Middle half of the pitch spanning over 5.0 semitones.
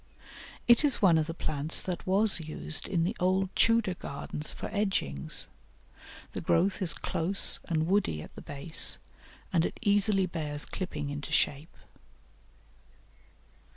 No: average, 4.2 semitones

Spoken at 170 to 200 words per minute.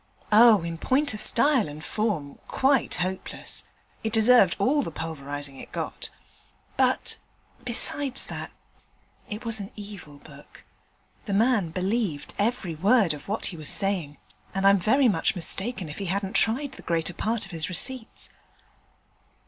No: average, 150 wpm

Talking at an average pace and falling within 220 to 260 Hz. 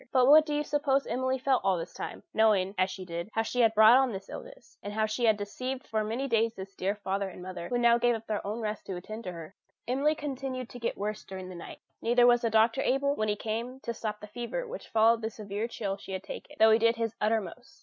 No: fast, 260 wpm; high, 225 Hz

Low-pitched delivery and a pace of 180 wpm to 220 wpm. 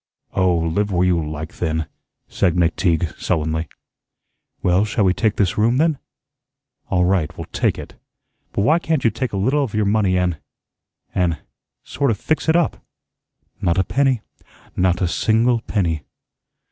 No: very low, 95 Hz; average, 160 wpm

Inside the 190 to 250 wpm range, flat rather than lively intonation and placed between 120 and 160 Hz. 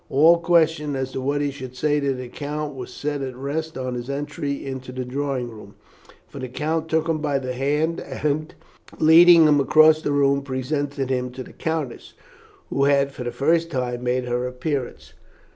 No: average, 195 wpm; average, 3.1 semitones; medium, 140 Hz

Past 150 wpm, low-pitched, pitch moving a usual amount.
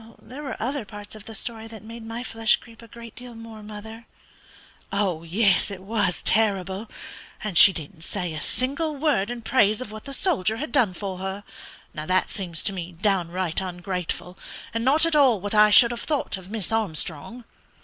No: average, 190 wpm; high, 215 Hz; average, 3.8 semitones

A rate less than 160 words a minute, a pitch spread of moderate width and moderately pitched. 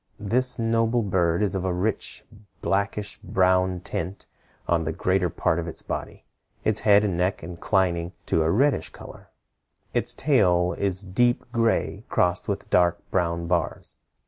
No: average, 150 wpm; average, 3.3 semitones; very low, 95 Hz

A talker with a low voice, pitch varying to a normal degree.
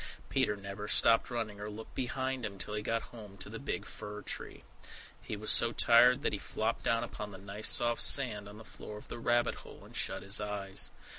No: low, 105 Hz; narrow, 2.3 semitones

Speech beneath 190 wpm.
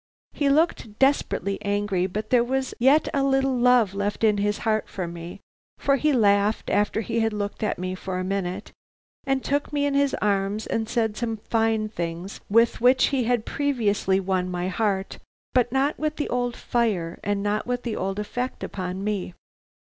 No: average, 195 wpm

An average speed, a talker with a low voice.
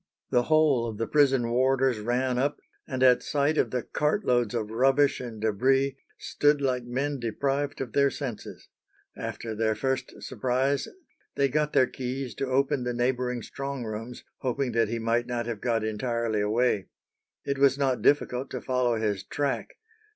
Yes: average, 170 wpm; low, 125 Hz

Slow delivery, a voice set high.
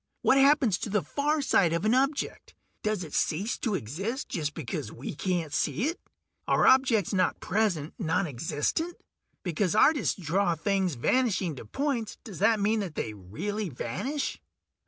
No: average, 155 wpm; high, 195 Hz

